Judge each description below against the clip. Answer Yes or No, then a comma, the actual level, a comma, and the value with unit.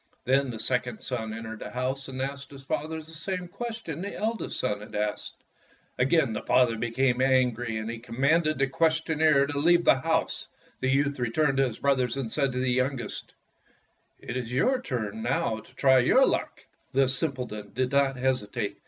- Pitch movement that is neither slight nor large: Yes, average, 3.2 semitones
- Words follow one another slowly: No, average, 190 wpm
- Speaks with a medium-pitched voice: No, low, 130 Hz